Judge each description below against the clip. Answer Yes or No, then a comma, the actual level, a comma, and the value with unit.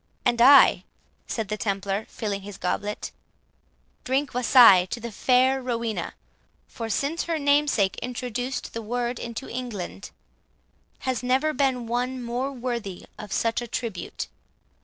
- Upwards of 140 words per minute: No, slow, 135 wpm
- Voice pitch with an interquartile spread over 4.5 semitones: No, average, 3.2 semitones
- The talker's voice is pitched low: No, high, 240 Hz